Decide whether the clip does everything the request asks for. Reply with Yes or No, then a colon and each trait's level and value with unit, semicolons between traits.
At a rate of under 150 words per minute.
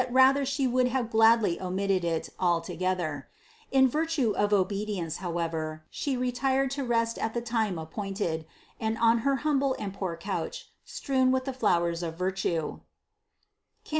No: average, 155 wpm